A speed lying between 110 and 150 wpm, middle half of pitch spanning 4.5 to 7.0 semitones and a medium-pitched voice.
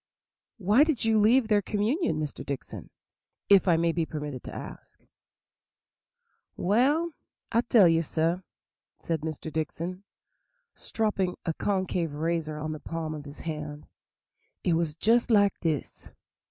Yes: average, 140 wpm; average, 5.2 semitones; medium, 170 Hz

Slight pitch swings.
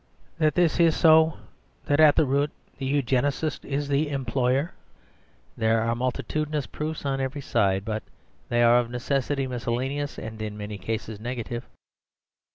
No: average, 3.7 semitones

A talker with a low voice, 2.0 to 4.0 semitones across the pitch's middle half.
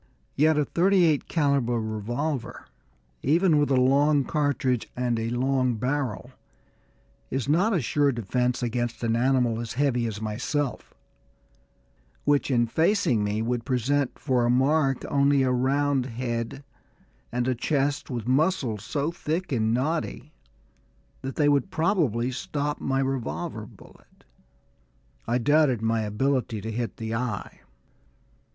Yes: low, 130 Hz; average, 3.5 semitones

